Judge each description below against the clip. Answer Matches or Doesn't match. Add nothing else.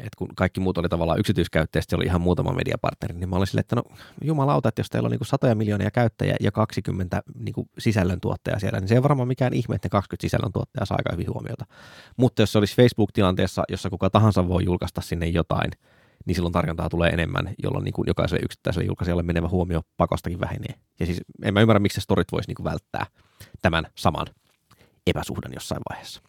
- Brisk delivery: Matches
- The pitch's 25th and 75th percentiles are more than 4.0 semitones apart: Matches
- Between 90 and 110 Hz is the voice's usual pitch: Matches